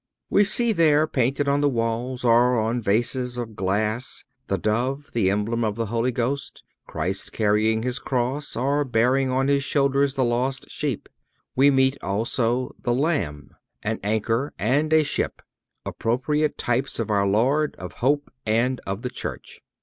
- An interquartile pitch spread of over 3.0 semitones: Yes, average, 3.7 semitones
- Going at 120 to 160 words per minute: Yes, average, 155 wpm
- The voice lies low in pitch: Yes, low, 125 Hz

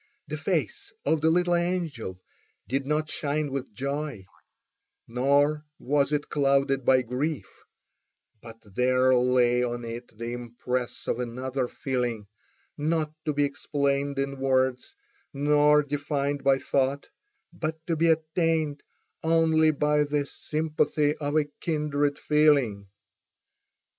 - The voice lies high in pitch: No, medium, 140 Hz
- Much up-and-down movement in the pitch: No, average, 3.0 semitones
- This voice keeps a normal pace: No, slow, 125 wpm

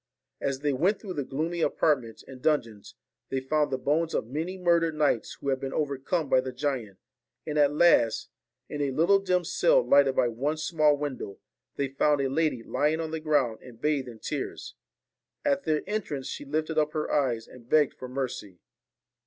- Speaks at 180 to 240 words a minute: Yes, average, 190 wpm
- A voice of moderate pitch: Yes, medium, 145 Hz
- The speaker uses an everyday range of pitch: Yes, average, 3.4 semitones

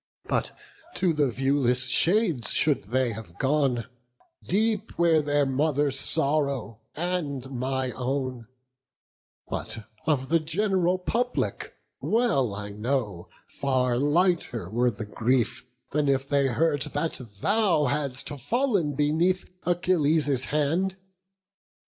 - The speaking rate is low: Yes, slow, 110 wpm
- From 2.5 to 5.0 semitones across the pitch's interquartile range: Yes, average, 4.7 semitones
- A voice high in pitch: No, medium, 140 Hz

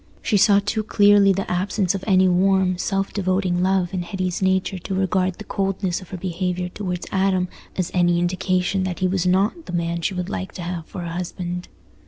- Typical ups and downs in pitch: No, narrow, 1.5 semitones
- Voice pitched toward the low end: No, medium, 185 Hz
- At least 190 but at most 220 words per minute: Yes, fast, 205 wpm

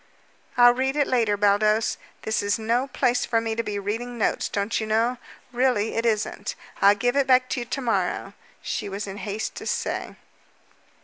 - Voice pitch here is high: Yes, high, 225 Hz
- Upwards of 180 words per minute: Yes, average, 190 wpm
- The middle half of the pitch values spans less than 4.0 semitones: Yes, average, 3.0 semitones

